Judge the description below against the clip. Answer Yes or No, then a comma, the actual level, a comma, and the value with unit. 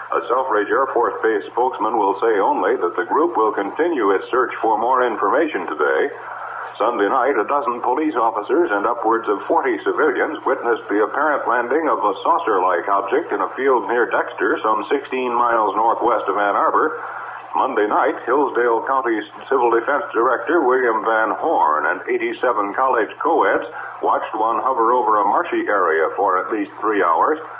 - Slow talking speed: No, average, 170 wpm